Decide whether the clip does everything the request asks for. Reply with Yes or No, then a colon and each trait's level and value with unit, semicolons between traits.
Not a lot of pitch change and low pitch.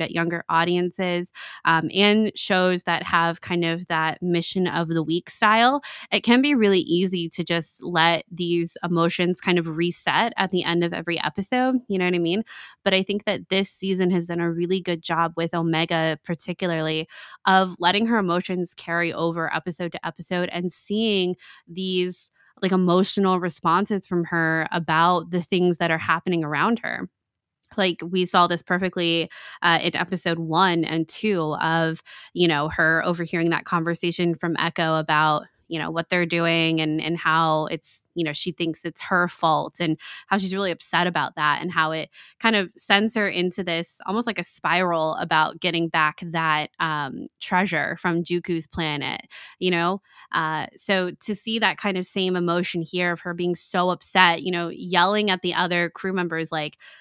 No: narrow, 1.9 semitones; medium, 175 Hz